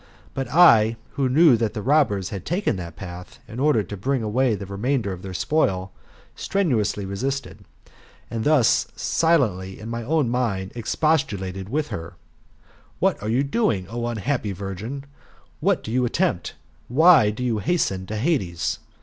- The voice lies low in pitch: Yes, low, 115 Hz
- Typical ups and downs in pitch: No, wide, 5.9 semitones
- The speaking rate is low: No, average, 160 wpm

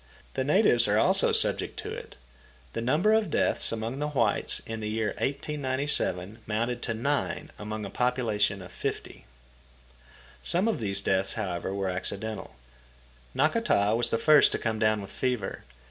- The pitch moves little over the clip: No, average, 4.3 semitones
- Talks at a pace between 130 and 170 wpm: Yes, average, 160 wpm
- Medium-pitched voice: No, low, 115 Hz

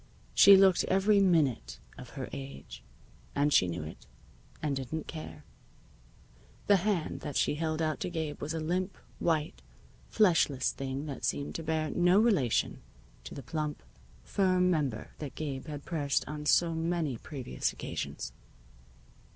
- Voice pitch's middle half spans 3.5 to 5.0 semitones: Yes, average, 4.1 semitones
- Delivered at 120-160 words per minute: Yes, average, 150 wpm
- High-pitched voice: No, medium, 155 Hz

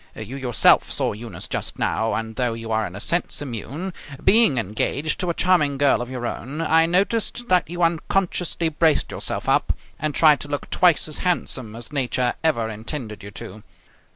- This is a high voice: No, medium, 140 Hz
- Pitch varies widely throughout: Yes, wide, 6.5 semitones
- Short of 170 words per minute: No, average, 185 wpm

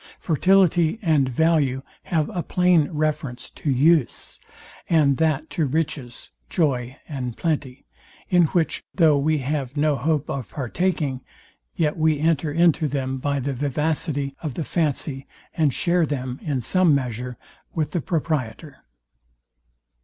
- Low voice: No, medium, 150 Hz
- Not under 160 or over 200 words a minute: No, slow, 135 wpm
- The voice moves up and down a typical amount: Yes, average, 3.3 semitones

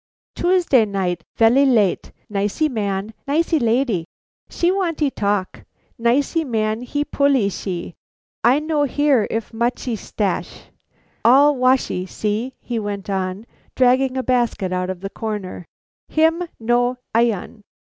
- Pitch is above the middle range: Yes, high, 235 Hz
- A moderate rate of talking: No, slow, 125 wpm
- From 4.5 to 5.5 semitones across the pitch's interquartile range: Yes, average, 5.2 semitones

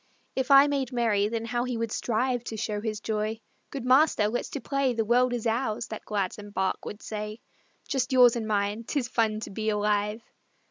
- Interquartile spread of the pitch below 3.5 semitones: Yes, average, 2.9 semitones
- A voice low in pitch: No, high, 225 Hz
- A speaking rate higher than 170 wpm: Yes, average, 200 wpm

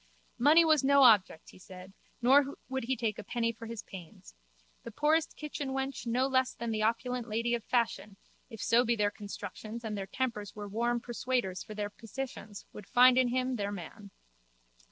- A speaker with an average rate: Yes, average, 185 wpm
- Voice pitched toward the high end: Yes, high, 235 Hz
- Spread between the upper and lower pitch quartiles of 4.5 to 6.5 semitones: No, average, 3.7 semitones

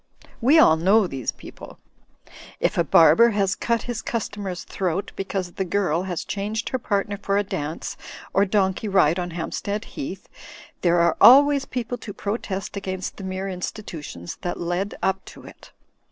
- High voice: Yes, high, 195 Hz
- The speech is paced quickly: No, average, 165 wpm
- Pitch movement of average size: Yes, average, 3.3 semitones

